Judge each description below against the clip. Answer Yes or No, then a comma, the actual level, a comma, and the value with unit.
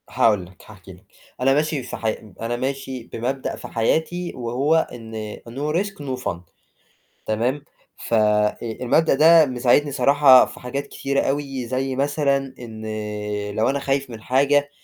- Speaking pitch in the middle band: No, low, 130 Hz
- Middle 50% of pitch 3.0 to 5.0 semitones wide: Yes, average, 3.6 semitones